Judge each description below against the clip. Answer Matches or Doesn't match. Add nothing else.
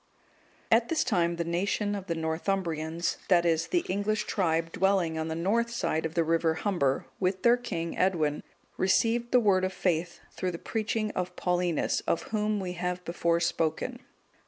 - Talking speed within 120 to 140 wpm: Doesn't match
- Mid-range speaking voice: Matches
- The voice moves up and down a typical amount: Matches